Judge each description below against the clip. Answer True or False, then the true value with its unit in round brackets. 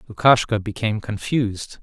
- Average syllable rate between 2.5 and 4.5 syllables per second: False (5.4 syllables/s)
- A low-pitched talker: True (105 Hz)